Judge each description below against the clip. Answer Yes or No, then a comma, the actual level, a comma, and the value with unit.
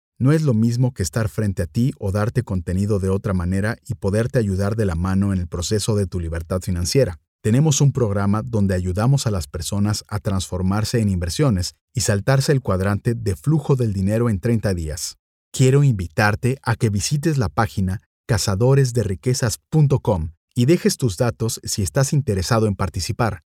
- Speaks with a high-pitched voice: No, low, 105 Hz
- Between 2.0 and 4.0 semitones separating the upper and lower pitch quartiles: No, average, 4.4 semitones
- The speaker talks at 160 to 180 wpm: Yes, average, 175 wpm